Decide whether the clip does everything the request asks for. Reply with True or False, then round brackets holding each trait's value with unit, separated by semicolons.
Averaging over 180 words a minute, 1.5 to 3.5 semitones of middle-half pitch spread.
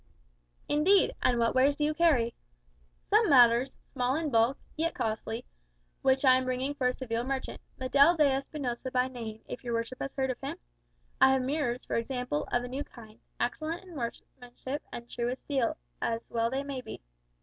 True (190 wpm; 2.8 semitones)